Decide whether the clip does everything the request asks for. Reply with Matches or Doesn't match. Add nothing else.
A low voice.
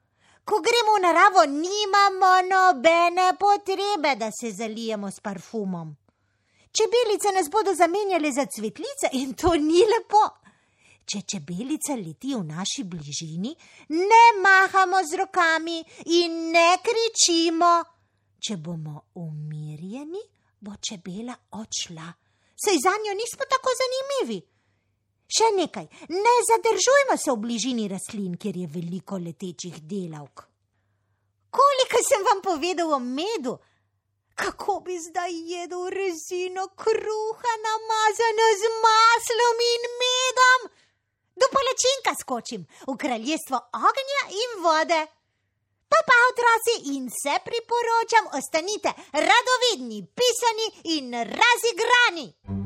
Doesn't match